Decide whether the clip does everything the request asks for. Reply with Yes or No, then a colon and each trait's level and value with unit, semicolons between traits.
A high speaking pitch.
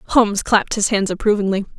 Yes: high, 205 Hz